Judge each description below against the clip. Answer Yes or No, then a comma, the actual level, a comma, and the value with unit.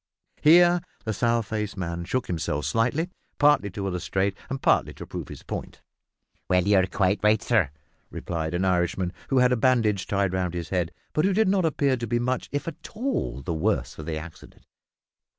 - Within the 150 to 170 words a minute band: No, average, 185 wpm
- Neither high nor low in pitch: No, low, 105 Hz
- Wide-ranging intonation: Yes, wide, 6.5 semitones